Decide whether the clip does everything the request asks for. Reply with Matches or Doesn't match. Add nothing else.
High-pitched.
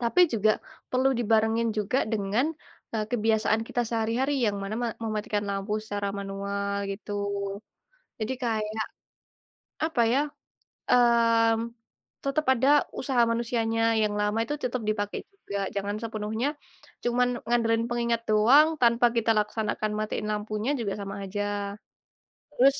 Matches